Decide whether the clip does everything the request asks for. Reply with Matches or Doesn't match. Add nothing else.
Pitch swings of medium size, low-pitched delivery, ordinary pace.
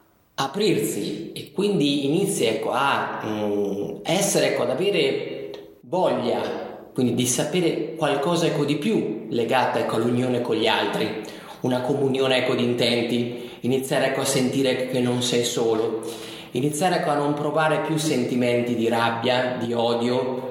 Matches